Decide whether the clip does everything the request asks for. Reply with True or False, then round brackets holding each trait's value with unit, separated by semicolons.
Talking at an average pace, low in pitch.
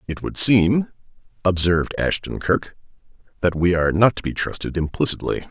True (155 wpm; 95 Hz)